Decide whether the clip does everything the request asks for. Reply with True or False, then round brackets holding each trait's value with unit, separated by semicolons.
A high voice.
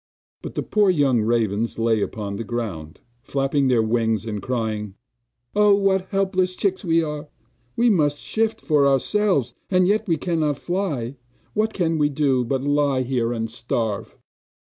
False (140 Hz)